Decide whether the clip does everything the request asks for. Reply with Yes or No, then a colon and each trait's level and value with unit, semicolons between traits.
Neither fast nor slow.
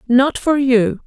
Yes: average, 170 wpm